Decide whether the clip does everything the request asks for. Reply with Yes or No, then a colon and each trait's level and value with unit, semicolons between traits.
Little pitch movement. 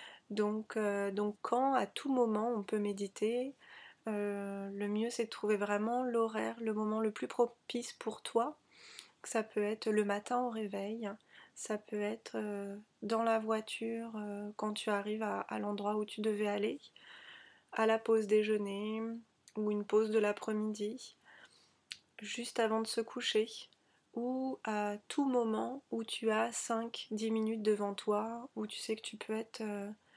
Yes: narrow, 1.5 semitones